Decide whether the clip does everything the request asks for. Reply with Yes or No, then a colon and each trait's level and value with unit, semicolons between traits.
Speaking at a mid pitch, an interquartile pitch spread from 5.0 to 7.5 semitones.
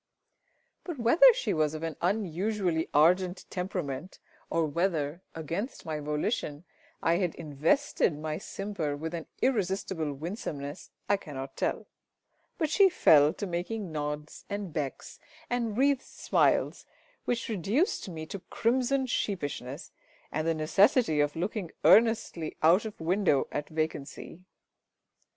Yes: medium, 170 Hz; wide, 5.4 semitones